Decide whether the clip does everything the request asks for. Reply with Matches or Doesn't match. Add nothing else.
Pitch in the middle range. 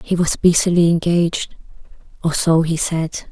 Matches